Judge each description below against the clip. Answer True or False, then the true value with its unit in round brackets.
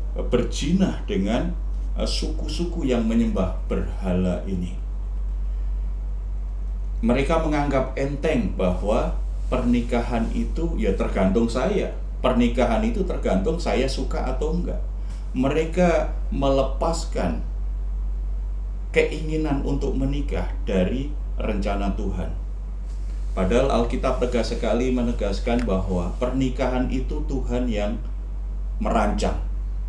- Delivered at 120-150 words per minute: False (85 wpm)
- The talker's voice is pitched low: True (120 Hz)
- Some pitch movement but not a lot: False (6.2 semitones)